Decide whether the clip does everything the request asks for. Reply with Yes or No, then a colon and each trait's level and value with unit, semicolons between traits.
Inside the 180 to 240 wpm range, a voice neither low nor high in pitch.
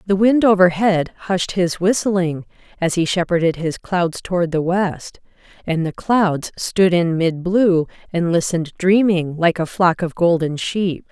No: average, 160 wpm; medium, 175 Hz